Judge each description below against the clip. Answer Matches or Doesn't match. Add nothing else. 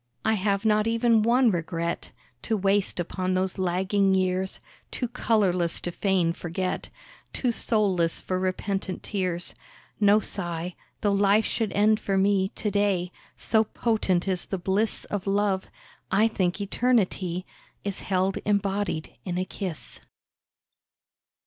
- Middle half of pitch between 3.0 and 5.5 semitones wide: Doesn't match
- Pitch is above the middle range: Matches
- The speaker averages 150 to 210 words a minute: Doesn't match